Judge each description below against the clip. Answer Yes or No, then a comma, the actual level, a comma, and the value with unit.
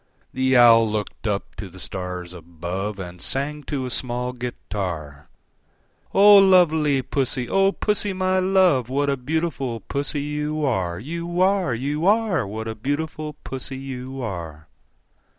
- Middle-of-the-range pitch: No, low, 130 Hz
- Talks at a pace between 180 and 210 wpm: No, average, 145 wpm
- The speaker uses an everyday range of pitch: No, wide, 6.9 semitones